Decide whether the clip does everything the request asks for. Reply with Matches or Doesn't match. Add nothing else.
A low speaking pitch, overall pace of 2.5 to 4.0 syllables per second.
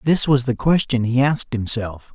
Doesn't match